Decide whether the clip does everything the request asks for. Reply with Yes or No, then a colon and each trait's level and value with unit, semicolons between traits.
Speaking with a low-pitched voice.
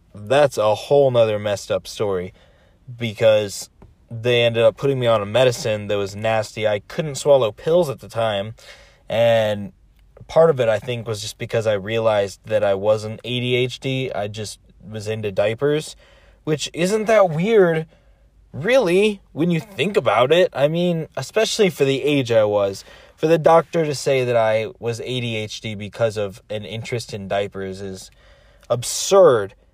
Yes: low, 115 Hz